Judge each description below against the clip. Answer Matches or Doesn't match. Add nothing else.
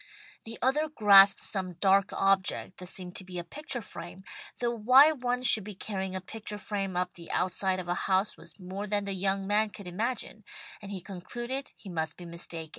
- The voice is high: Matches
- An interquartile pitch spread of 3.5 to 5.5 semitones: Doesn't match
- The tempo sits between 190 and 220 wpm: Matches